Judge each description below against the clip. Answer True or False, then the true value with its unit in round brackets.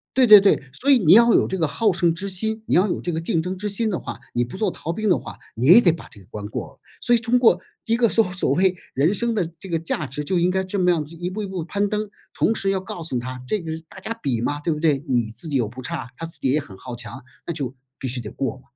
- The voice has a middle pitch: True (170 Hz)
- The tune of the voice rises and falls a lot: True (6.4 semitones)